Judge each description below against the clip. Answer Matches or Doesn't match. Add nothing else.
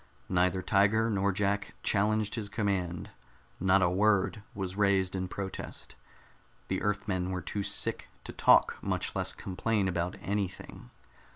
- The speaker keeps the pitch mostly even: Matches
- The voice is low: Matches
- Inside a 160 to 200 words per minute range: Doesn't match